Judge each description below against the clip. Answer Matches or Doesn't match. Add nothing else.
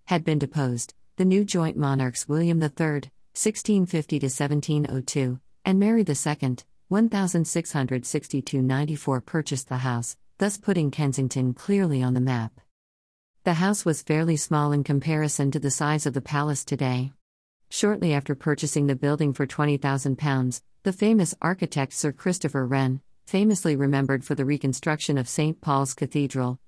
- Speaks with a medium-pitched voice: Matches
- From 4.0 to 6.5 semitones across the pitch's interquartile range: Doesn't match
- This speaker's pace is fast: Doesn't match